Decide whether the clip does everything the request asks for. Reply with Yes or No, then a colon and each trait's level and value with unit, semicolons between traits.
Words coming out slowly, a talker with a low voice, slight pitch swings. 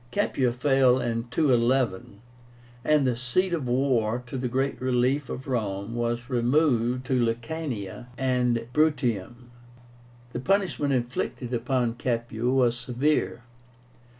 Yes: slow, 120 wpm; low, 125 Hz; narrow, 2.0 semitones